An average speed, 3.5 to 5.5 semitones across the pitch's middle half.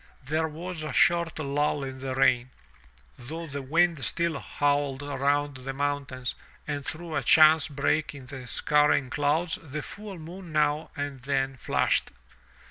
No: average, 150 wpm; average, 2.7 semitones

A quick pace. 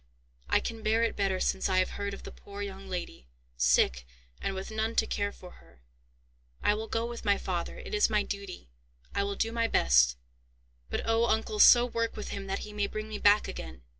Yes: fast, 220 wpm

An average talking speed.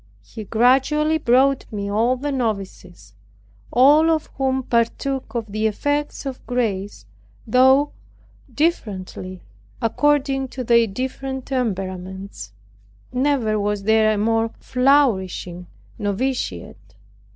No: slow, 105 wpm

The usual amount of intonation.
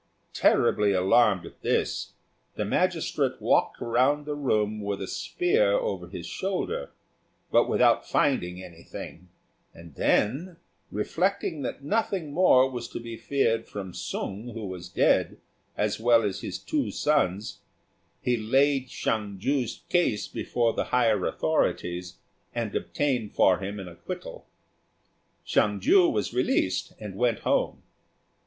No: wide, 6.4 semitones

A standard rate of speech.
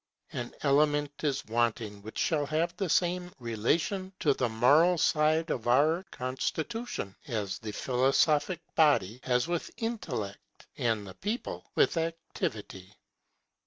No: slow, 125 wpm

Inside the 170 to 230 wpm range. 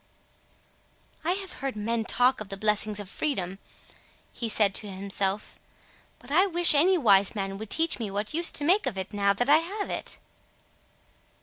Yes: average, 180 wpm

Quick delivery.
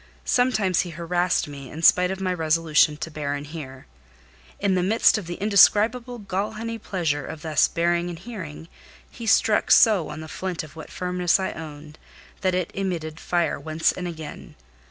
No: average, 180 wpm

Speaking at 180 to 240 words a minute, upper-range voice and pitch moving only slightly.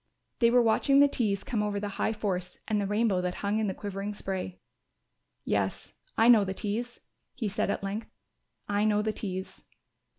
Yes: average, 190 wpm; high, 210 Hz; narrow, 2.1 semitones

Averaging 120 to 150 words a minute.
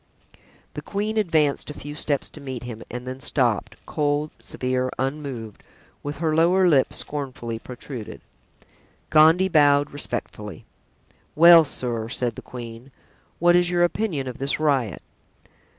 Yes: slow, 135 wpm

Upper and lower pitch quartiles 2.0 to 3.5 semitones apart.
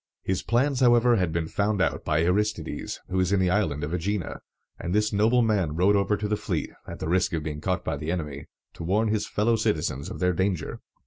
No: average, 4.3 semitones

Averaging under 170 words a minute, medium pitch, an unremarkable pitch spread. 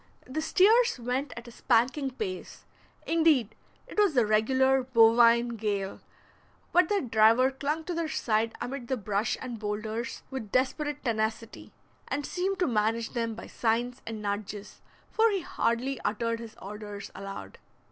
No: average, 150 wpm; high, 235 Hz; average, 3.9 semitones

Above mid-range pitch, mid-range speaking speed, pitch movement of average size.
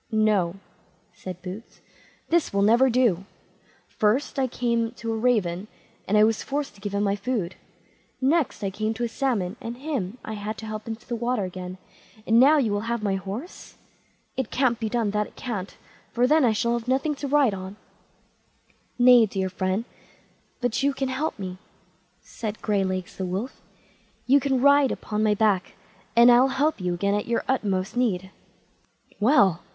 Yes: high, 220 Hz; average, 180 wpm; average, 4.1 semitones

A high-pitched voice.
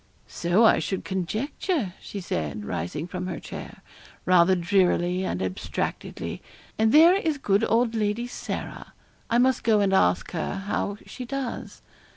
Yes: high, 200 Hz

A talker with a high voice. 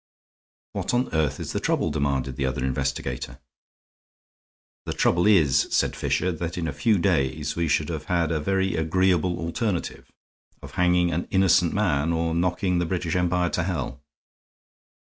No: very low, 85 Hz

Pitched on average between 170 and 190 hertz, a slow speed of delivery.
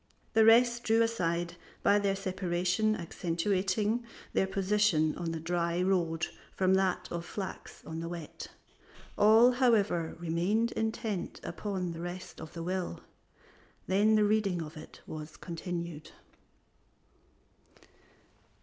Yes: medium, 185 Hz; slow, 120 wpm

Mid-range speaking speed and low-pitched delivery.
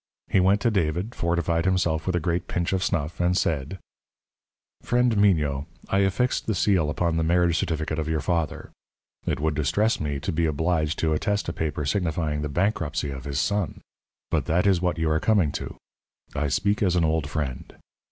Yes: average, 190 wpm; very low, 85 Hz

